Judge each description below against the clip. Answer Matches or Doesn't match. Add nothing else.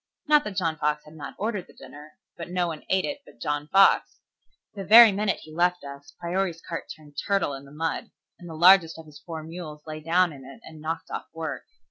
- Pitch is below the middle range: Doesn't match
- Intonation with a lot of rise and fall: Doesn't match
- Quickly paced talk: Matches